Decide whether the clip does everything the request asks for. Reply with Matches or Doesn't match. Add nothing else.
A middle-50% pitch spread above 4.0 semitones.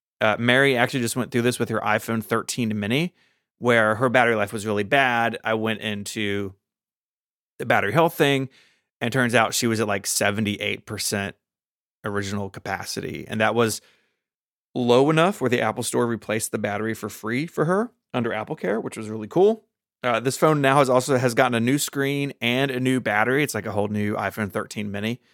Doesn't match